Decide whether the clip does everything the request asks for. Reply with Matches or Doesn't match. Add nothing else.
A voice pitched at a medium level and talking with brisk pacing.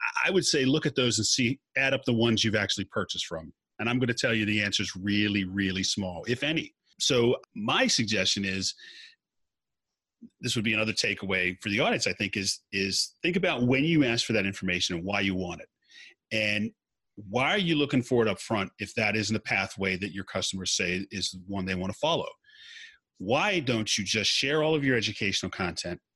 Doesn't match